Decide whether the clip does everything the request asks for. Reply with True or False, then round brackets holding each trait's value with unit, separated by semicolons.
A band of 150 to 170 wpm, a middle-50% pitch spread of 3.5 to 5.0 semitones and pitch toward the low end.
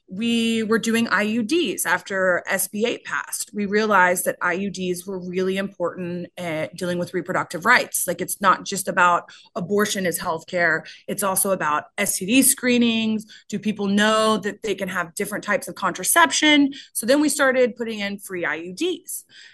False (160 wpm; 4.1 semitones; 200 Hz)